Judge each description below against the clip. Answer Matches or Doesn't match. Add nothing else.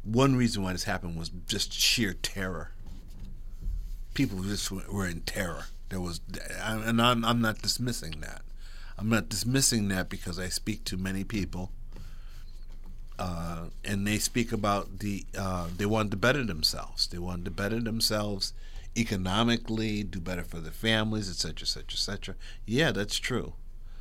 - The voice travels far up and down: Doesn't match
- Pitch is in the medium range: Doesn't match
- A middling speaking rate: Matches